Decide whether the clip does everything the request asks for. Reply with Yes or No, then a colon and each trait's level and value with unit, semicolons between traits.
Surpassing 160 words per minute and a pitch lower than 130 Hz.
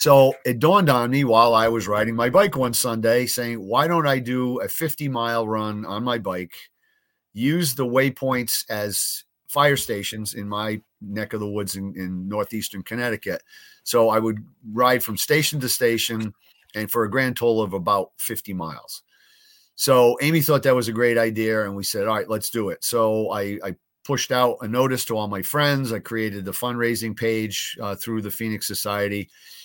Yes: average, 190 wpm; low, 115 Hz